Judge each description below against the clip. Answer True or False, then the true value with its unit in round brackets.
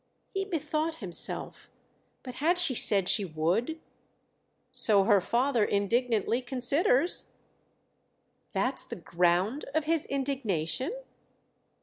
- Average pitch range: False (7.2 semitones)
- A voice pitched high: True (250 Hz)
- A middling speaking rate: False (100 wpm)